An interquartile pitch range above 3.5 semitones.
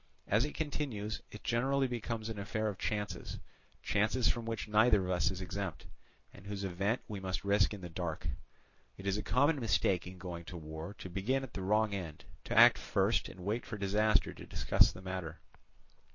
No: average, 3.1 semitones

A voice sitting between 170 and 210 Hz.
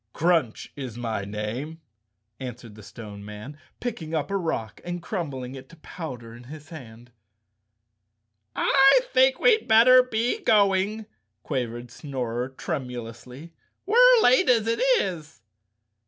No: medium, 145 Hz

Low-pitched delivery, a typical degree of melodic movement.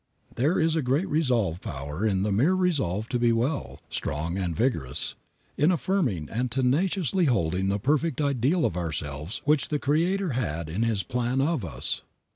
No: low, 125 Hz; wide, 8.4 semitones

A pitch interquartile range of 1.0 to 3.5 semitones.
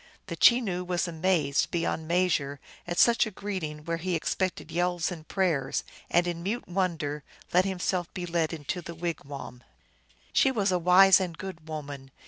Yes: average, 2.7 semitones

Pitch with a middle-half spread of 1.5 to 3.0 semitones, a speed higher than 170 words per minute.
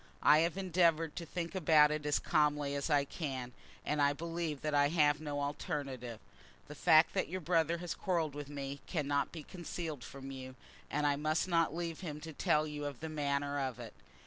Yes: narrow, 2.6 semitones; average, 200 wpm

